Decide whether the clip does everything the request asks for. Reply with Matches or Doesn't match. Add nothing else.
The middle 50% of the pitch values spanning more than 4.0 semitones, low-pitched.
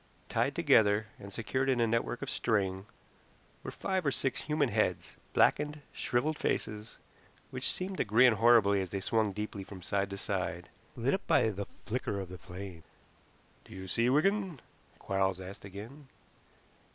Matches